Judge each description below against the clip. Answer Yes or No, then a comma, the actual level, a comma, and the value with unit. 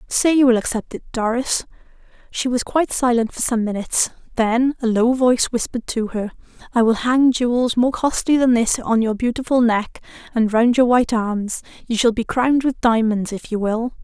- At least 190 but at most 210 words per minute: Yes, average, 195 wpm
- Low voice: No, high, 240 Hz